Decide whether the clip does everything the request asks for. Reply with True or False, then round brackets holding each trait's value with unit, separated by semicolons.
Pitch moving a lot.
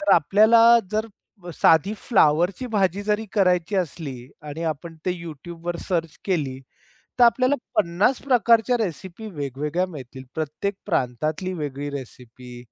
True (6.2 semitones)